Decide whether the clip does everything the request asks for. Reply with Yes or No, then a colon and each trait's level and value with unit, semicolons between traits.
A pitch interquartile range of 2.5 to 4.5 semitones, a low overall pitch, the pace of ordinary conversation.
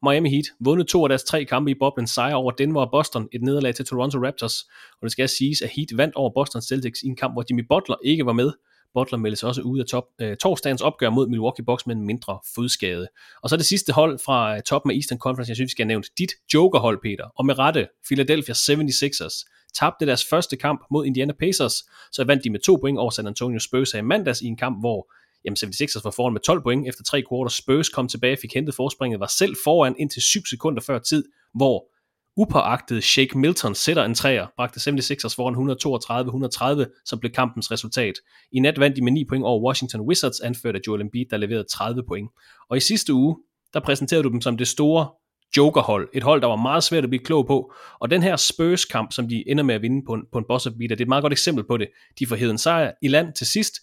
No: average, 3.2 semitones; low, 130 Hz; fast, 240 wpm